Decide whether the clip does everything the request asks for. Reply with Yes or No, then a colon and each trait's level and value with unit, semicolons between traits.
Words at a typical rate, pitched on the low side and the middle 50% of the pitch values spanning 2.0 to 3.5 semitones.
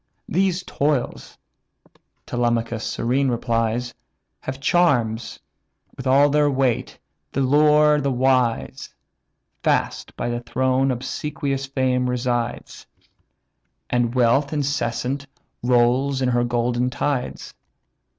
No: slow, 90 wpm; low, 130 Hz; narrow, 2.6 semitones